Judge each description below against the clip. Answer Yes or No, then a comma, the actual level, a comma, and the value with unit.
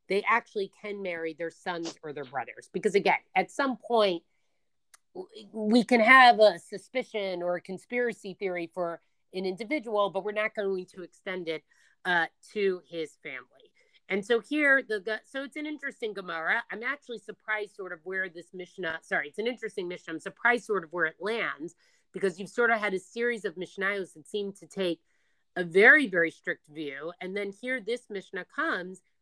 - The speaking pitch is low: No, high, 195 Hz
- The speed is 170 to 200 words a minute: Yes, average, 185 wpm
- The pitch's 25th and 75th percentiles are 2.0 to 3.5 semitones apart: No, average, 4.0 semitones